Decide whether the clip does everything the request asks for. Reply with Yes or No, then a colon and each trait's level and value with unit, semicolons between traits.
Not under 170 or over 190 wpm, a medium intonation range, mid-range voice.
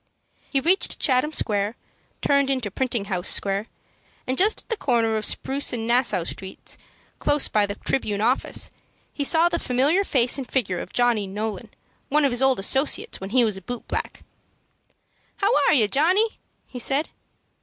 No: average, 175 wpm; average, 4.9 semitones; very high, 250 Hz